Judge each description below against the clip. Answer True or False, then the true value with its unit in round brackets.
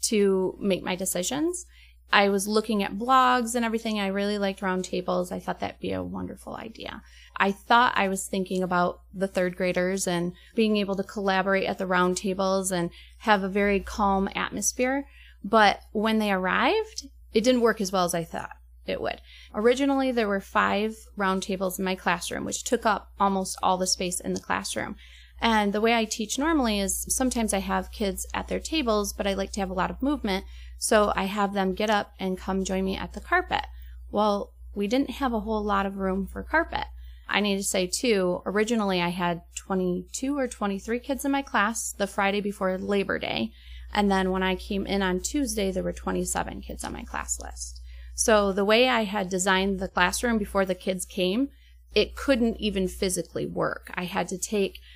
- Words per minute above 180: True (200 wpm)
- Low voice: False (195 Hz)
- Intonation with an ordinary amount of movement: True (3.0 semitones)